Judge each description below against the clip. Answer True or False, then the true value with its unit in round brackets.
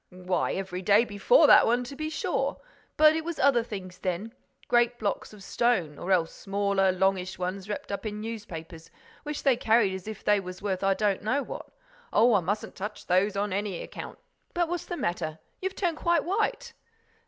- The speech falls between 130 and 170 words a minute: False (185 wpm)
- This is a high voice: True (205 Hz)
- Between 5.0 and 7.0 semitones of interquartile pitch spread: False (4.6 semitones)